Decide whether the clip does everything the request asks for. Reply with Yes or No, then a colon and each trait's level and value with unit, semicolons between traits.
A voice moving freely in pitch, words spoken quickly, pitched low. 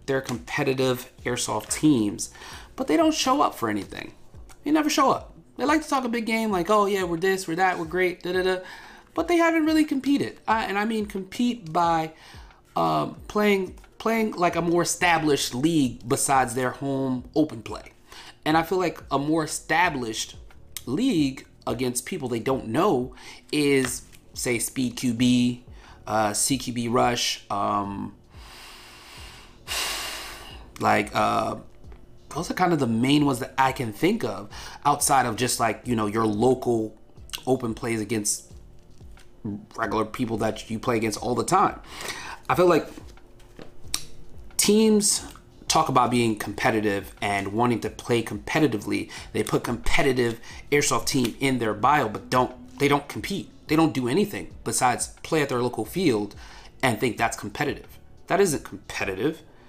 No: wide, 6.8 semitones; average, 155 wpm; low, 130 Hz